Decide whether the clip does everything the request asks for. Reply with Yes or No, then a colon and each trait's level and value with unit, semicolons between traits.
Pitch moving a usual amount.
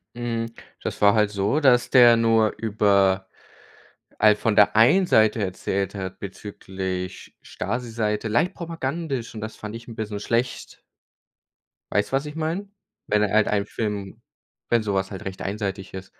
Yes: average, 3.0 semitones